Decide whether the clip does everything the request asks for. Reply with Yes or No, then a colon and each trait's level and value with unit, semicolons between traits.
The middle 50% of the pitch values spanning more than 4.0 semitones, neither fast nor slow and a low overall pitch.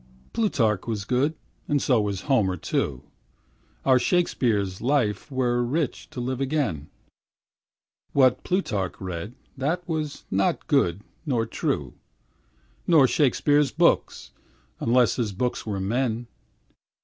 No: wide, 5.6 semitones; slow, 115 wpm; low, 125 Hz